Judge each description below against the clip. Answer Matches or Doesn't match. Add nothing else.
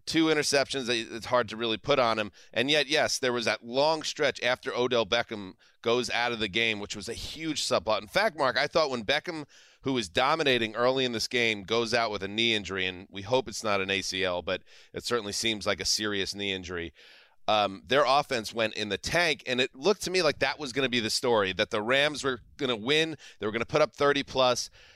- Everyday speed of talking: Doesn't match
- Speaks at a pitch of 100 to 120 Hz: Matches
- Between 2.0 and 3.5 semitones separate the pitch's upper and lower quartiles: Doesn't match